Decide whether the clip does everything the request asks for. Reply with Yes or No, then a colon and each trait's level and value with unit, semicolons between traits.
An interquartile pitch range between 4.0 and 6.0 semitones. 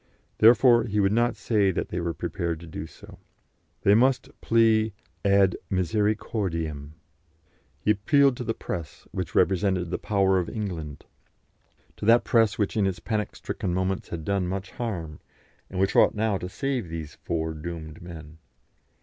Yes: average, 4.5 semitones